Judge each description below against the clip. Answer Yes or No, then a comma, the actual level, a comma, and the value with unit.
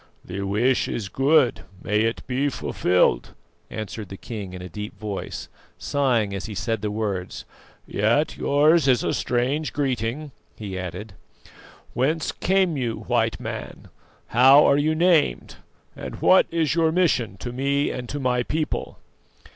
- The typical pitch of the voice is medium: No, low, 125 Hz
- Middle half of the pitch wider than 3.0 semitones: Yes, wide, 5.5 semitones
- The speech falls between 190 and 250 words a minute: No, average, 150 wpm